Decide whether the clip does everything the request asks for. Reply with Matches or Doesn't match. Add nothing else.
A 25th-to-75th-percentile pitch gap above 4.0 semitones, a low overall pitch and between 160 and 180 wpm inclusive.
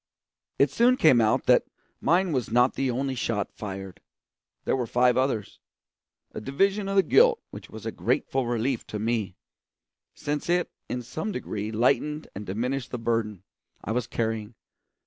Matches